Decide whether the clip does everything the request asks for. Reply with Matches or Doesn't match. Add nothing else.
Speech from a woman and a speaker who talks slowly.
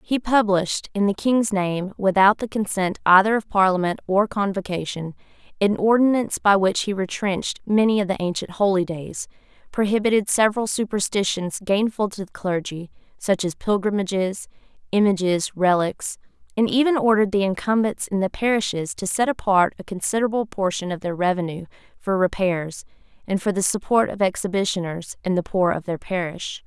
Doesn't match